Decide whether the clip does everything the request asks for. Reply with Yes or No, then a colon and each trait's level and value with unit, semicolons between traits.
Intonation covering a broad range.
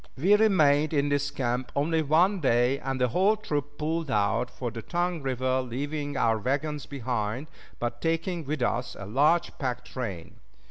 No: average, 4.1 semitones